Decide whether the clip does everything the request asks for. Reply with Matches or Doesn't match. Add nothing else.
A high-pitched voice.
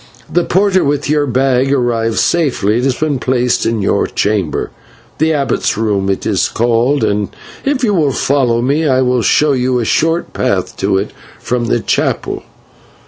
Doesn't match